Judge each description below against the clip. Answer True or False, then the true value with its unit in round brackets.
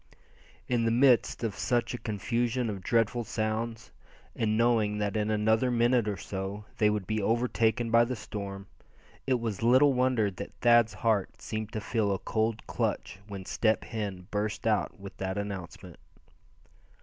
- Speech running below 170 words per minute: True (160 wpm)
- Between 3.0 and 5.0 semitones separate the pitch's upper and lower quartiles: False (2.4 semitones)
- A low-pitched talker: True (110 Hz)